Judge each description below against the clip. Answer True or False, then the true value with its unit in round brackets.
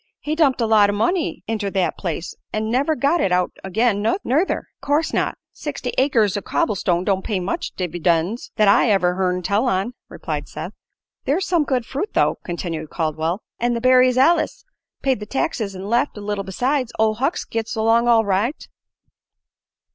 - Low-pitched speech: False (220 Hz)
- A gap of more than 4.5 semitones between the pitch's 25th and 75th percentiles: True (5.3 semitones)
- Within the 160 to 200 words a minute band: True (180 wpm)